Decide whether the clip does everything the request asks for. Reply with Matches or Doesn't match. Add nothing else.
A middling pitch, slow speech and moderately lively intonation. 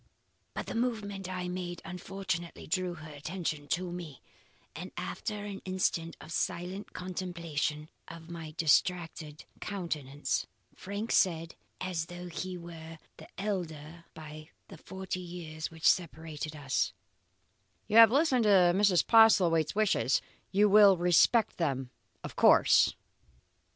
Matches